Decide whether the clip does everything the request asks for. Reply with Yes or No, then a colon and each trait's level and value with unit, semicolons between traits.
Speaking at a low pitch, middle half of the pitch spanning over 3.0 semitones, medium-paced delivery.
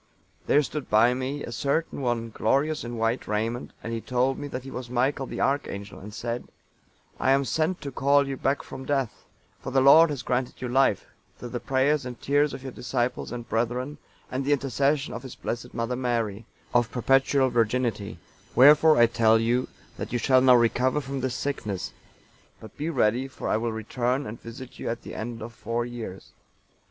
No: low, 125 Hz; average, 2.7 semitones; average, 195 wpm